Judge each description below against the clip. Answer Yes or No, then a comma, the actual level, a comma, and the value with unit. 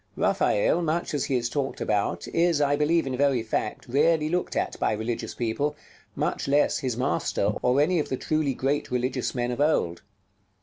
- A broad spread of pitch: No, average, 3.8 semitones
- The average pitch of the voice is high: No, low, 135 Hz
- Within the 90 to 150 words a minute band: No, average, 185 wpm